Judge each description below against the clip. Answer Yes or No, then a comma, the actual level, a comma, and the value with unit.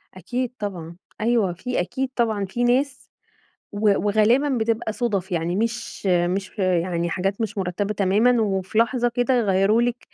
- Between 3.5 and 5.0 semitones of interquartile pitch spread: Yes, average, 4.3 semitones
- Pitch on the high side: Yes, high, 210 Hz